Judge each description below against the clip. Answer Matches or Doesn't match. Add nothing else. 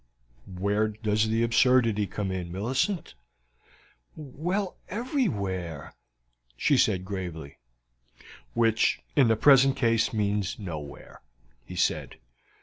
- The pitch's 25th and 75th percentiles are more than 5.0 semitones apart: Matches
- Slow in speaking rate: Matches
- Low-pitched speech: Matches